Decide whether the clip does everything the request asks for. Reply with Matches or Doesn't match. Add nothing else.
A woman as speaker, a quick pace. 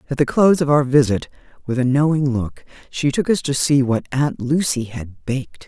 Matches